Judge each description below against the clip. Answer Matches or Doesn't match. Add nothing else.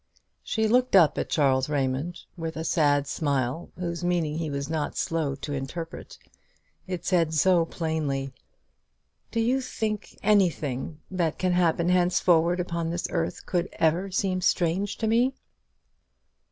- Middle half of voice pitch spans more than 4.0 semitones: Doesn't match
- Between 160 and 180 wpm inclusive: Doesn't match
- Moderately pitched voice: Matches